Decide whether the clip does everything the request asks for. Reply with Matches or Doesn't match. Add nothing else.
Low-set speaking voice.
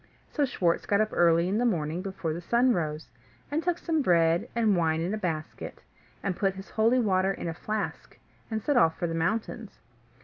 Doesn't match